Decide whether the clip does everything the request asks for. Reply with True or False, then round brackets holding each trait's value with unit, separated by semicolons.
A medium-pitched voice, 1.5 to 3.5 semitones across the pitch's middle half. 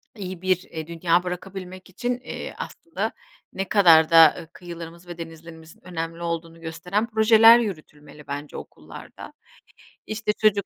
True (175 Hz; 3.1 semitones)